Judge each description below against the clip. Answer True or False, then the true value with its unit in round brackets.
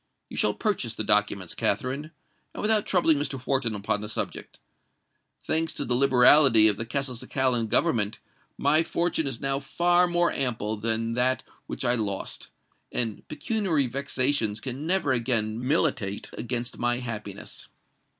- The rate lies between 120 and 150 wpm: True (140 wpm)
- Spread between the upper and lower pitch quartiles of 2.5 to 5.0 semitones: True (4.6 semitones)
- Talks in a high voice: False (125 Hz)